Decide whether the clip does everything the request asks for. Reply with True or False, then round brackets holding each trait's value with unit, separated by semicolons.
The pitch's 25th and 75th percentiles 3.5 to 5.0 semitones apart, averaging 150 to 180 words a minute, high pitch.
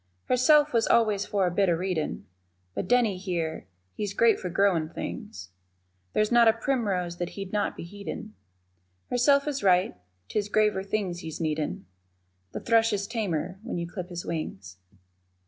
True (4.5 semitones; 165 wpm; 195 Hz)